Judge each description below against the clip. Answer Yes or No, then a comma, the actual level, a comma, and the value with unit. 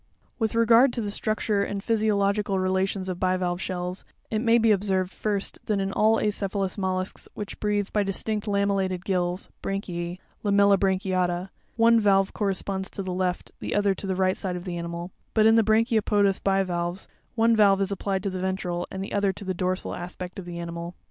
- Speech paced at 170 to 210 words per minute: Yes, average, 185 wpm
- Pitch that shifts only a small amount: Yes, narrow, 2.0 semitones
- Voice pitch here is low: No, high, 195 Hz